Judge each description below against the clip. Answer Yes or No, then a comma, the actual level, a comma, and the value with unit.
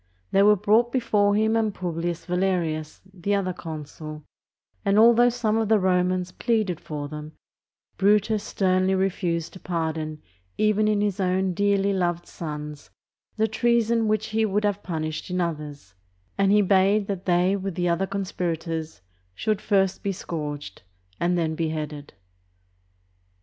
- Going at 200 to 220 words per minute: No, average, 145 wpm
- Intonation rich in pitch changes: No, average, 3.9 semitones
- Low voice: No, medium, 185 Hz